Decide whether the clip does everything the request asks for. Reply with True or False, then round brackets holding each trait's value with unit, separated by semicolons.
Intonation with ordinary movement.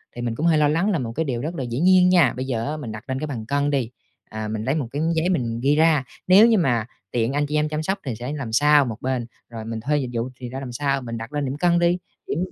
True (4.4 semitones)